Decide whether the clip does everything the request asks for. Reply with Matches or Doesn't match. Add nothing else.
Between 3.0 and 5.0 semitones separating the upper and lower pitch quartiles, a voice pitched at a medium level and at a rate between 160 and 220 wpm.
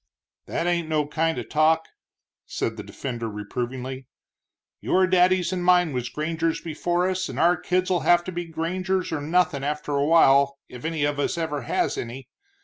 Matches